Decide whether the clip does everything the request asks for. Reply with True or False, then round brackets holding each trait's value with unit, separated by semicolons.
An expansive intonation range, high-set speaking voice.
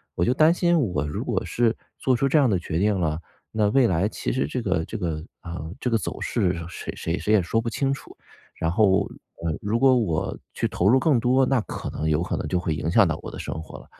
False (6.9 semitones; 100 Hz)